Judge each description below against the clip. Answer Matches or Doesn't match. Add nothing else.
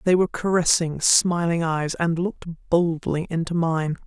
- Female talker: Matches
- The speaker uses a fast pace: Doesn't match